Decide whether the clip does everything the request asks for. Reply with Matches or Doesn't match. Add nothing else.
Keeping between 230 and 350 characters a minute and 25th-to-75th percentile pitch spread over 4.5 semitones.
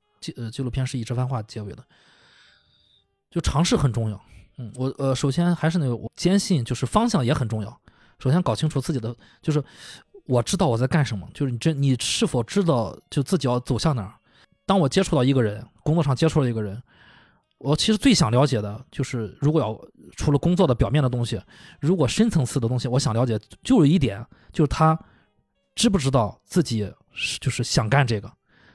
Matches